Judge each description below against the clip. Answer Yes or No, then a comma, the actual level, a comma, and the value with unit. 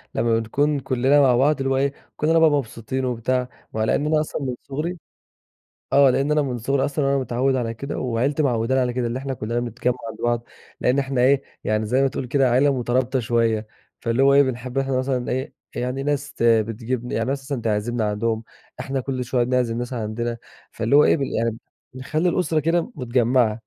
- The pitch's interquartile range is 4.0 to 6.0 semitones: No, average, 2.7 semitones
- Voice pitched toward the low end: Yes, low, 130 Hz